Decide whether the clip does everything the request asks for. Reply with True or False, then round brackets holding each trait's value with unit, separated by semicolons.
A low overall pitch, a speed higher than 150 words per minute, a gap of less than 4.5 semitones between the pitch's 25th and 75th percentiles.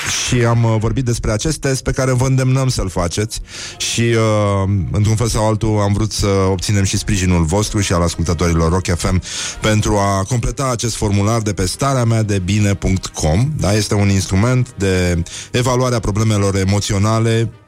True (105 Hz; 165 wpm; 3.3 semitones)